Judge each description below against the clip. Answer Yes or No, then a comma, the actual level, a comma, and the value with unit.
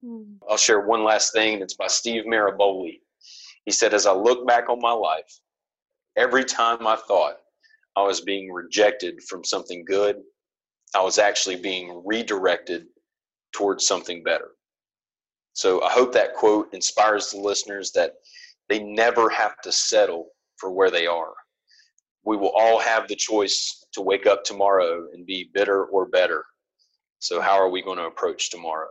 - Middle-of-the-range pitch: No, low, 110 Hz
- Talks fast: No, average, 160 wpm